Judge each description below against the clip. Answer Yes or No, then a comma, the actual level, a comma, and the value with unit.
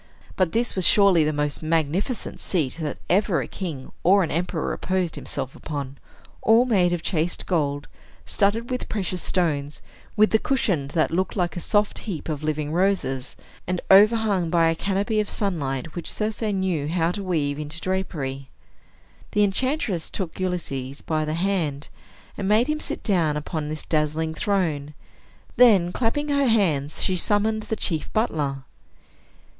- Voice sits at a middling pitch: Yes, medium, 175 Hz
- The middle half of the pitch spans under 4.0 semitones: No, average, 5.0 semitones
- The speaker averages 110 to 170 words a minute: Yes, average, 160 wpm